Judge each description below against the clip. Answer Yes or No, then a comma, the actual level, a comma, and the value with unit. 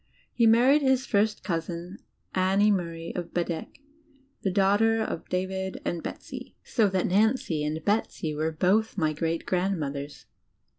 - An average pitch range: Yes, average, 4.3 semitones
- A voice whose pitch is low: No, medium, 185 Hz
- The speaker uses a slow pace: No, average, 145 wpm